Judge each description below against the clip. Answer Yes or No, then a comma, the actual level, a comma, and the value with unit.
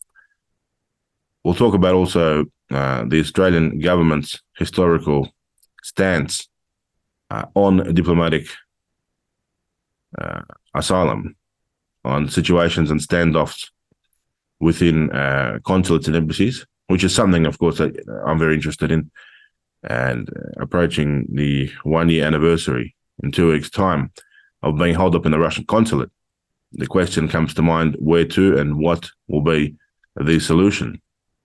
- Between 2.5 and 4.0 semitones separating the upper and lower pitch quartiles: Yes, average, 2.9 semitones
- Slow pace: Yes, slow, 120 wpm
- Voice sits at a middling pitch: No, very low, 80 Hz